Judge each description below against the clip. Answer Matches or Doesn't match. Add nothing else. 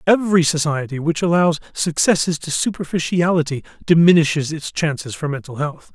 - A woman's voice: Doesn't match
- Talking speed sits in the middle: Doesn't match